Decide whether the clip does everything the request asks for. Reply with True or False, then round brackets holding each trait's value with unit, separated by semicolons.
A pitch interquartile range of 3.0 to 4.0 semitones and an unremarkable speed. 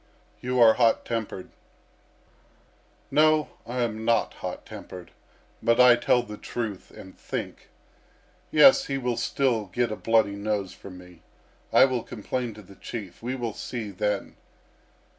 True (3.4 semitones; 145 wpm)